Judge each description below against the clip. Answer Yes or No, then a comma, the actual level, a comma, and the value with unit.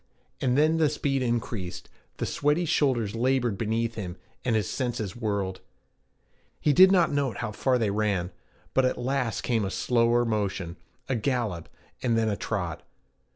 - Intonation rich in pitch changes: No, average, 4.2 semitones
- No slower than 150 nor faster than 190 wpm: Yes, average, 160 wpm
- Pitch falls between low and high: No, low, 115 Hz